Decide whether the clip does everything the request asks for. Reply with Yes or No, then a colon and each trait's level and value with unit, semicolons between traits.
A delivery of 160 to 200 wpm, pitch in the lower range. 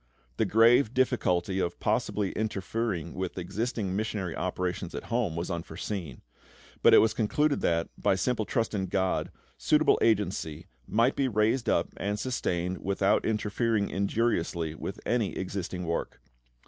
No: average, 140 wpm; low, 100 Hz